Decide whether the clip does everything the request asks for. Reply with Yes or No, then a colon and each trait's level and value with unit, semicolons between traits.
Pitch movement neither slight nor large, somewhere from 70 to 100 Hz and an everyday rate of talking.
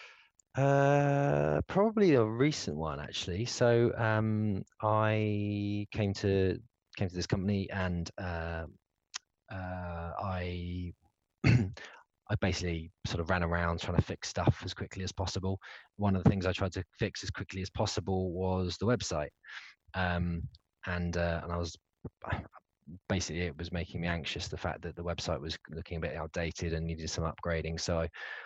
Yes: average, 3.3 semitones; very low, 90 Hz; average, 160 wpm